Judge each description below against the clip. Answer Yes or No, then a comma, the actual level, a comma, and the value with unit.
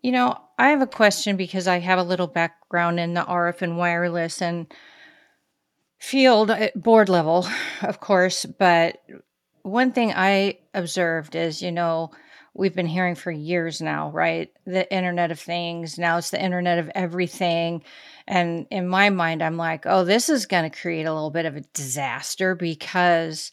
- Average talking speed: Yes, average, 170 wpm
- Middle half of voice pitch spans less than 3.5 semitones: Yes, narrow, 2.6 semitones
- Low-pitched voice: No, medium, 175 Hz